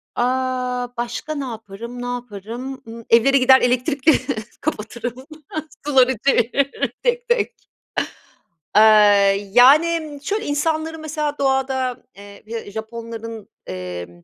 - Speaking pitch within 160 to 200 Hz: No, very high, 250 Hz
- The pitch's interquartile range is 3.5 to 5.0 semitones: Yes, average, 3.8 semitones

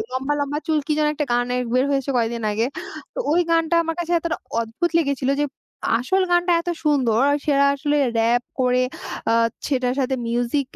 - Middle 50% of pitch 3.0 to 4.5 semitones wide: Yes, average, 4.1 semitones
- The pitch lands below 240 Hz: No, very high, 280 Hz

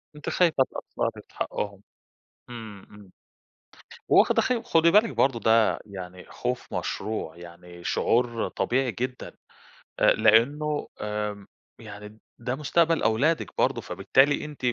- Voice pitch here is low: Yes, low, 115 Hz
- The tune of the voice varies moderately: No, wide, 5.9 semitones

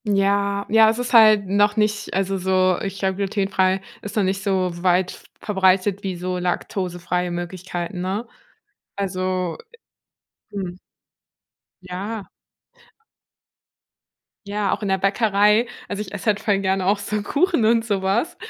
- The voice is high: Yes, high, 195 Hz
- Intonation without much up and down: Yes, narrow, 2.1 semitones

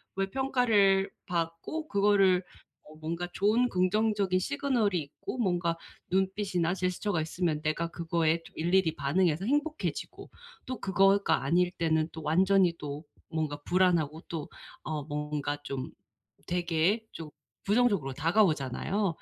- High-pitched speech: No, medium, 180 Hz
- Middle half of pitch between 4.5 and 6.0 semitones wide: No, average, 4.0 semitones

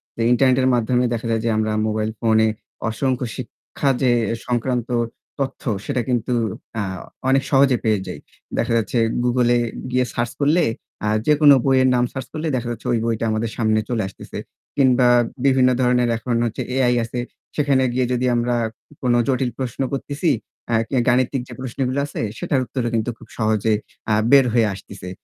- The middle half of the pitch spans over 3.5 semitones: No, narrow, 2.5 semitones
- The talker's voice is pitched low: Yes, low, 125 Hz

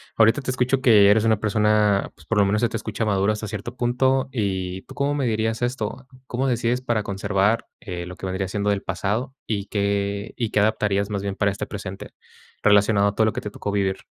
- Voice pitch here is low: Yes, low, 105 Hz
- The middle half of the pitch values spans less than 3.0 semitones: Yes, narrow, 2.6 semitones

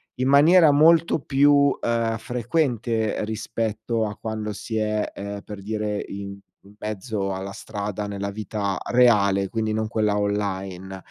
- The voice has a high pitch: No, low, 110 Hz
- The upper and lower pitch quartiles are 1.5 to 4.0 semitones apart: Yes, narrow, 2.5 semitones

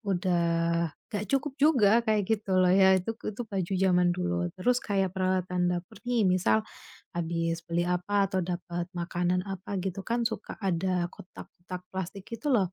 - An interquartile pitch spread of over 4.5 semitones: No, narrow, 2.5 semitones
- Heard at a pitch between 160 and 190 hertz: Yes, medium, 185 Hz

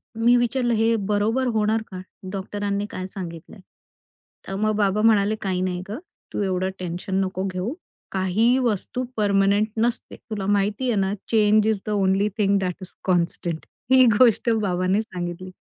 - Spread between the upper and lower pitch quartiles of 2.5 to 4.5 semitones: Yes, average, 2.8 semitones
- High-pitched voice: Yes, high, 205 Hz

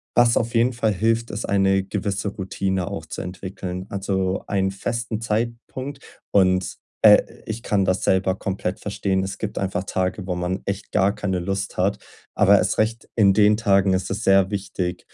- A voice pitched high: No, low, 100 Hz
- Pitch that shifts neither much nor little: No, narrow, 2.2 semitones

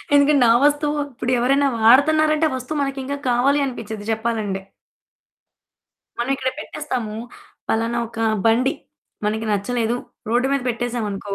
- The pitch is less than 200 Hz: No, high, 245 Hz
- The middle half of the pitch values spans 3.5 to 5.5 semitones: Yes, average, 3.8 semitones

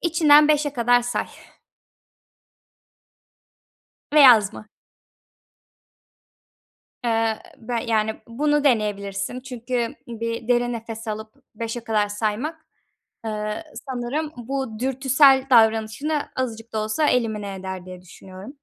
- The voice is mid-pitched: No, high, 230 Hz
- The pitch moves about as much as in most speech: Yes, average, 3.5 semitones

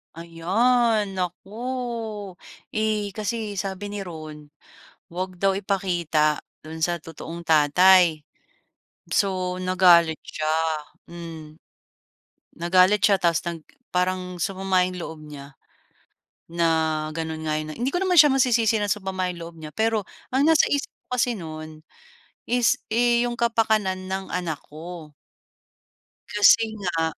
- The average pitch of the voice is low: No, medium, 185 Hz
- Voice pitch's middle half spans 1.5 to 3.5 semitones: No, average, 4.2 semitones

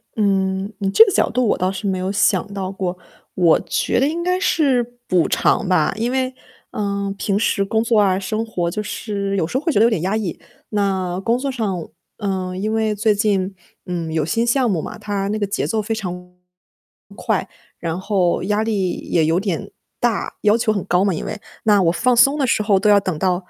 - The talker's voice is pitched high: Yes, high, 200 Hz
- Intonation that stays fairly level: No, average, 3.1 semitones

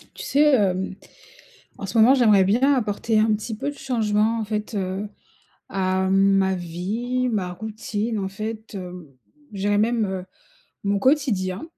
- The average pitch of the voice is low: No, high, 210 Hz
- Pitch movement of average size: Yes, average, 3.1 semitones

